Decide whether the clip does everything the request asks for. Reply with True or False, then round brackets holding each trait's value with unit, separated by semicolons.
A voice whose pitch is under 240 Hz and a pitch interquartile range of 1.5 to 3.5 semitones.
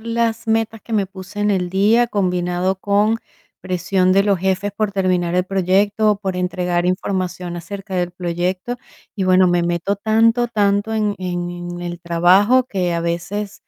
True (190 Hz; 2.7 semitones)